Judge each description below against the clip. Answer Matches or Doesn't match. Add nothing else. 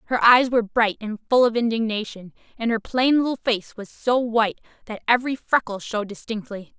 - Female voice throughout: Matches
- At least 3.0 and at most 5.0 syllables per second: Doesn't match